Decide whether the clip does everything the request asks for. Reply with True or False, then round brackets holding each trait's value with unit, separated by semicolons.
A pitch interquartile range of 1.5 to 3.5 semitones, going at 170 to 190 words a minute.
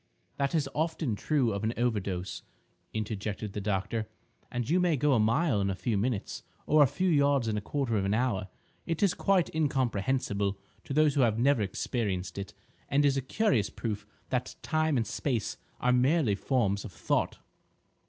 False (5.6 semitones; 185 wpm)